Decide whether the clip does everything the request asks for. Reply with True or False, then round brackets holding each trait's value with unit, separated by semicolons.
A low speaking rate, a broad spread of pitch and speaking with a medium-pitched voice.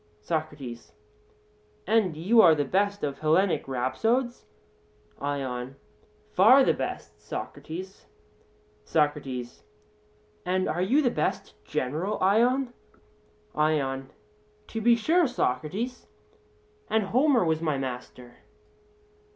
True (100 wpm; 8.3 semitones; 165 Hz)